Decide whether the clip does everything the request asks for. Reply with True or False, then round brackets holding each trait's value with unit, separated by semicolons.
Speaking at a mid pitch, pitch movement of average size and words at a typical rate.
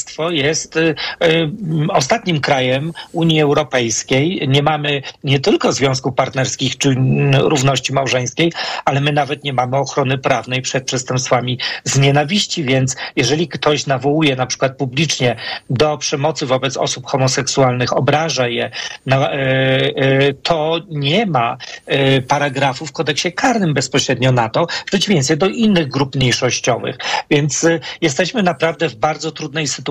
True (145 Hz; 3.2 semitones; 140 wpm)